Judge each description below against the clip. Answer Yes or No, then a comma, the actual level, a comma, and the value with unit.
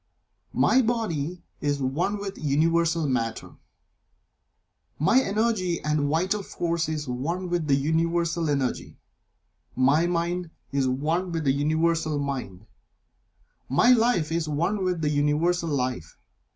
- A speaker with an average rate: No, slow, 125 wpm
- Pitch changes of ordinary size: Yes, average, 3.5 semitones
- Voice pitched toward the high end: No, medium, 160 Hz